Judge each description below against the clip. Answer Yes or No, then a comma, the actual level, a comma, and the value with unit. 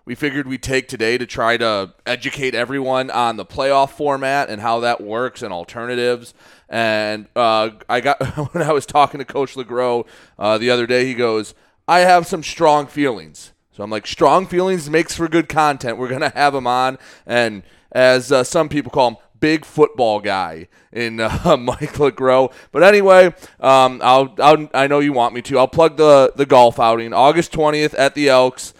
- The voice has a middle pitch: No, low, 130 Hz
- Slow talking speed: No, average, 190 wpm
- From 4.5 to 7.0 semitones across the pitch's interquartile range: No, average, 3.6 semitones